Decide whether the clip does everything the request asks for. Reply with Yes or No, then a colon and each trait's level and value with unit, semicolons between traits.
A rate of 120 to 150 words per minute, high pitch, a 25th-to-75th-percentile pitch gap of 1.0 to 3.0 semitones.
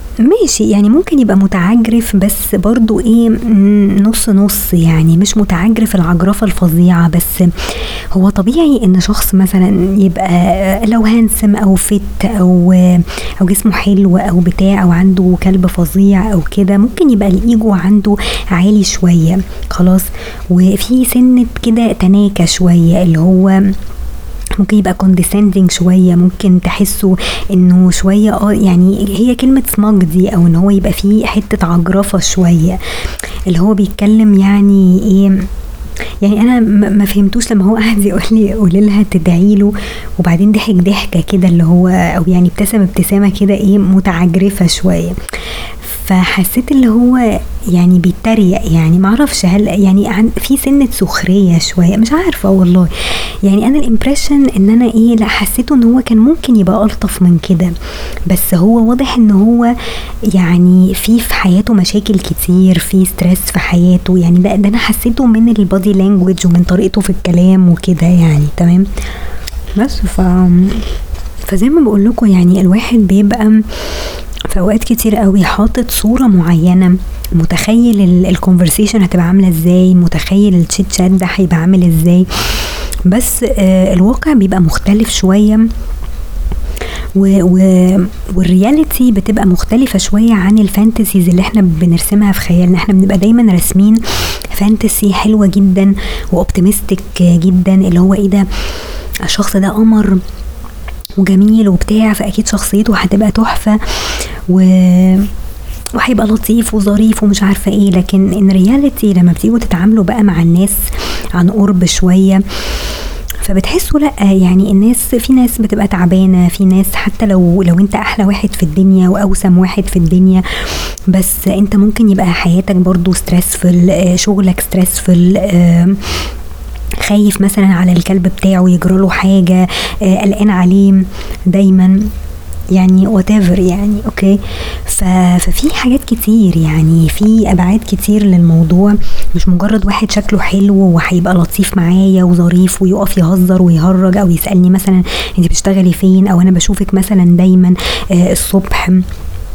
Yes: average, 130 wpm; high, 195 Hz; narrow, 2.5 semitones